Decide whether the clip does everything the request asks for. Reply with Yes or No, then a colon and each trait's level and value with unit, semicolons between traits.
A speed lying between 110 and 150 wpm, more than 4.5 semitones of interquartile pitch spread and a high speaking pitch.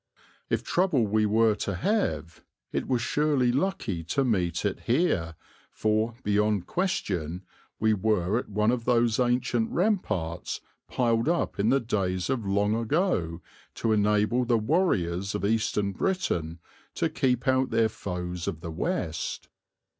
No: average, 145 wpm; average, 5.1 semitones; low, 110 Hz